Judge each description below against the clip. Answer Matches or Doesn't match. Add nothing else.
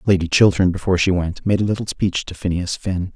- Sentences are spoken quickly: Matches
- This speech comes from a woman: Doesn't match